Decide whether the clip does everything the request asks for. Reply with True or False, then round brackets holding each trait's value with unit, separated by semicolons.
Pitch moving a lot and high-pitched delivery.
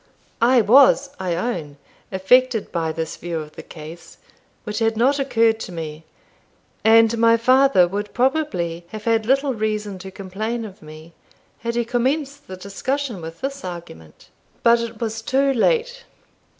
True (6.1 semitones; 225 Hz)